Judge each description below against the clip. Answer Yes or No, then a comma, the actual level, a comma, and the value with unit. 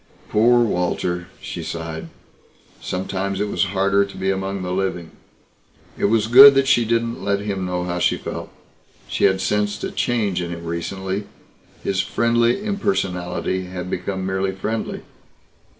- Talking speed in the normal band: Yes, average, 150 wpm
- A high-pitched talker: No, very low, 95 Hz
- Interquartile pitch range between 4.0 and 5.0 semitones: No, average, 3.3 semitones